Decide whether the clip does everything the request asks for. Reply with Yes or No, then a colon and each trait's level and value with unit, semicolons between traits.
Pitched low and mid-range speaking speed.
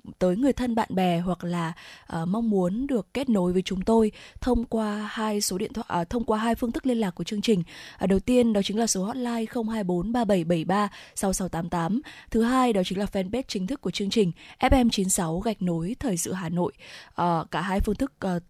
No: high, 205 Hz; average, 215 wpm